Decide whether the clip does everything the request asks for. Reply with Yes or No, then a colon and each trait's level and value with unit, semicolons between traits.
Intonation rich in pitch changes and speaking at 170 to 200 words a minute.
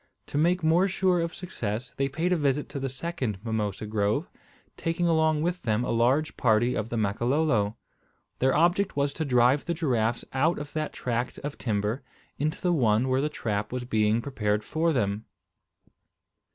Yes: wide, 6.1 semitones; average, 180 wpm